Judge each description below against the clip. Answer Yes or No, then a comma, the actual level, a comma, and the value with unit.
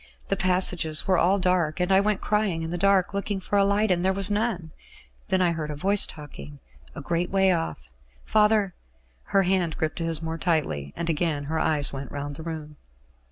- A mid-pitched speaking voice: Yes, medium, 175 Hz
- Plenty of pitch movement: No, average, 3.8 semitones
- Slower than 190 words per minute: No, fast, 205 wpm